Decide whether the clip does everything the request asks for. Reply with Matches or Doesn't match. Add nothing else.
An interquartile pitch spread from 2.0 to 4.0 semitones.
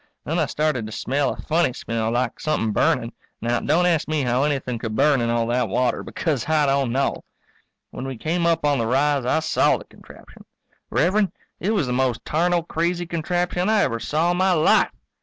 Doesn't match